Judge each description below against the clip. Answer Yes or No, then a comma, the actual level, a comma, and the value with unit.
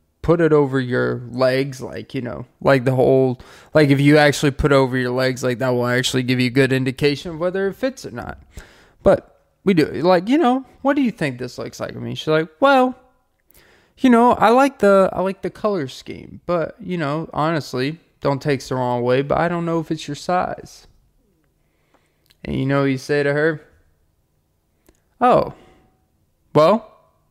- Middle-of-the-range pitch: Yes, medium, 145 Hz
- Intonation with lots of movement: Yes, wide, 5.8 semitones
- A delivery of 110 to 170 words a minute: No, average, 200 wpm